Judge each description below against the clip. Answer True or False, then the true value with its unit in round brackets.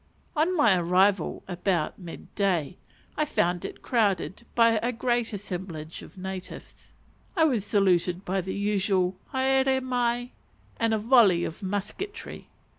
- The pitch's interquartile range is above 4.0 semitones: True (4.8 semitones)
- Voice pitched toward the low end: False (200 Hz)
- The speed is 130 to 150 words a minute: True (135 wpm)